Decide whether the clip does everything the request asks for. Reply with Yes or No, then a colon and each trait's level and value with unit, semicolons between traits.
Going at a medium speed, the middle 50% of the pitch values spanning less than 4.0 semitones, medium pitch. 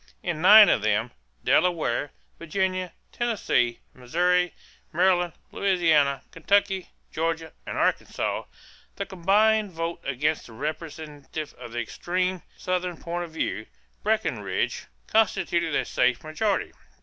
No: slow, 115 wpm; average, 3.5 semitones; medium, 170 Hz